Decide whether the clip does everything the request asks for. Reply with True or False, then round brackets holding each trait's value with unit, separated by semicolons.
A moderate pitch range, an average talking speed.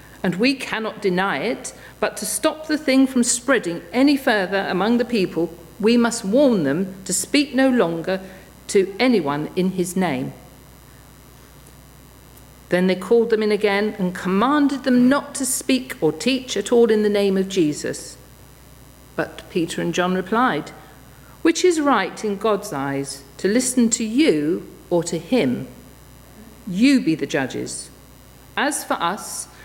False (6.4 semitones; 155 wpm)